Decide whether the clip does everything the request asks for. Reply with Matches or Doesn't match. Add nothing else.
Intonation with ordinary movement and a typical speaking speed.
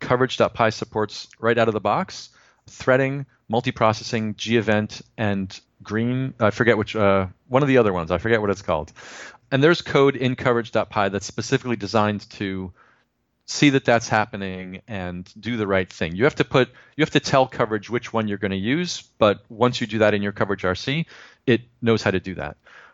Matches